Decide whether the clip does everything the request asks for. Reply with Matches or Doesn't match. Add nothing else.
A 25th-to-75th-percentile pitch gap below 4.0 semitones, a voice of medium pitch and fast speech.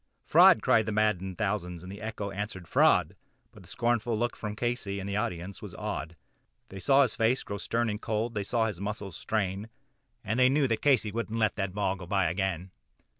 Doesn't match